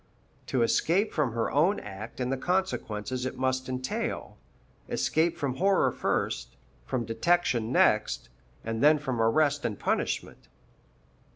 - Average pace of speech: No, slow, 130 wpm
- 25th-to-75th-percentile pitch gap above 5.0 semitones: Yes, wide, 5.4 semitones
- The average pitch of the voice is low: Yes, low, 130 Hz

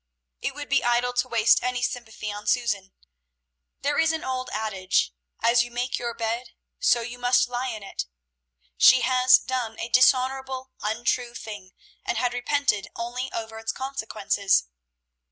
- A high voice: Yes, high, 240 Hz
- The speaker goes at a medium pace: Yes, average, 155 wpm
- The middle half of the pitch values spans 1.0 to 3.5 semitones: Yes, narrow, 2.4 semitones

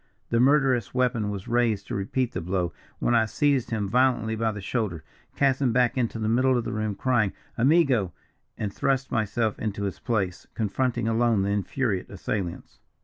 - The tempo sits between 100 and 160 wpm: No, average, 180 wpm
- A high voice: No, low, 115 Hz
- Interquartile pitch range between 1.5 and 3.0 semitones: No, average, 3.7 semitones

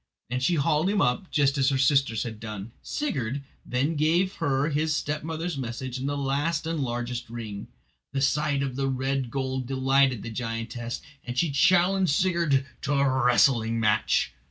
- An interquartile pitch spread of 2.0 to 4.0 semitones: Yes, average, 3.6 semitones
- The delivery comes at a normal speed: Yes, average, 170 wpm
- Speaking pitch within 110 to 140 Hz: Yes, low, 135 Hz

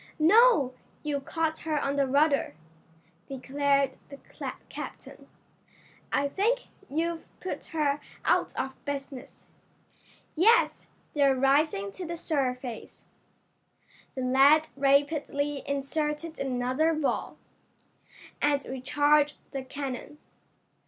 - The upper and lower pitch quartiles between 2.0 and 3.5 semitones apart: Yes, narrow, 2.4 semitones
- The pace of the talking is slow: Yes, slow, 100 wpm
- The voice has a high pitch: Yes, very high, 285 Hz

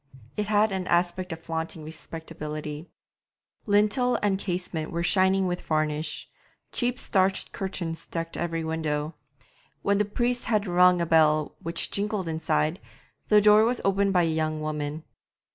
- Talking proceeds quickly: No, average, 145 wpm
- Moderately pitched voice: Yes, medium, 175 Hz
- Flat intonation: No, average, 3.8 semitones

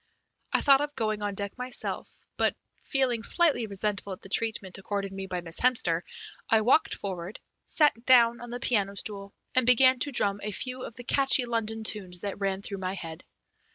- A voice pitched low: No, high, 215 Hz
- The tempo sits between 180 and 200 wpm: Yes, average, 190 wpm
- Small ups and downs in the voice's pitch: No, average, 4.1 semitones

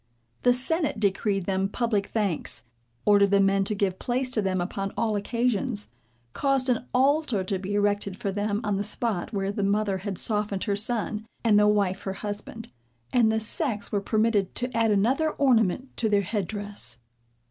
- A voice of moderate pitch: No, high, 210 Hz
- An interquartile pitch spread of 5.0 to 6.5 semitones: No, average, 2.8 semitones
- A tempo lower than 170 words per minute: No, average, 180 wpm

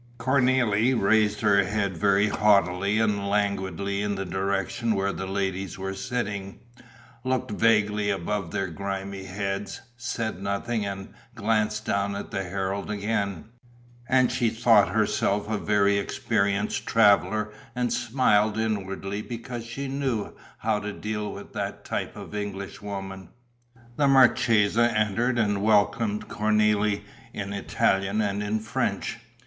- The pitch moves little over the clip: Yes, narrow, 2.1 semitones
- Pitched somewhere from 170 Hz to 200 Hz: No, low, 105 Hz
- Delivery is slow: Yes, slow, 130 wpm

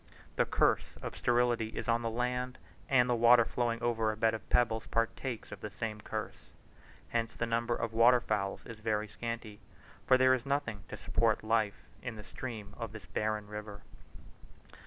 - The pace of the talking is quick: No, average, 180 wpm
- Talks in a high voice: No, low, 115 Hz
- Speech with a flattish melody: Yes, narrow, 1.9 semitones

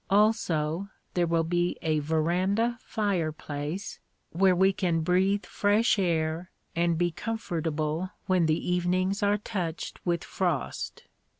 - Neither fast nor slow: No, slow, 120 wpm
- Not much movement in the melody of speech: No, average, 3.2 semitones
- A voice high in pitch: No, medium, 175 Hz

